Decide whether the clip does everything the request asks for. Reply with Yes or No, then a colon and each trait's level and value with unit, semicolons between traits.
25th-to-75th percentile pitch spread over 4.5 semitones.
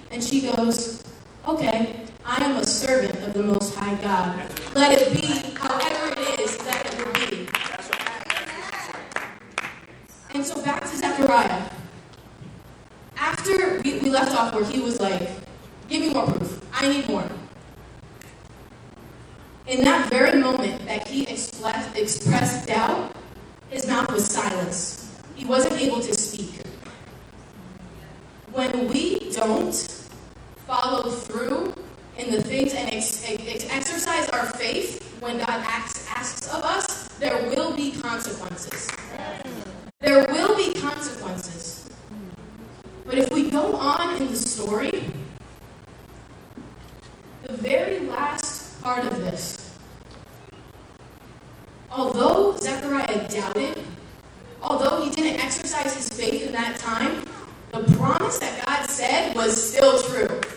No: average, 3.9 semitones